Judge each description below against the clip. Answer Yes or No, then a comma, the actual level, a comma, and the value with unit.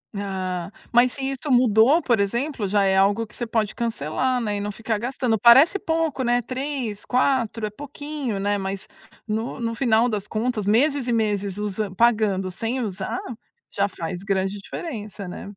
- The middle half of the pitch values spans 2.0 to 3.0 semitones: No, average, 3.8 semitones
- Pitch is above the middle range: Yes, high, 220 Hz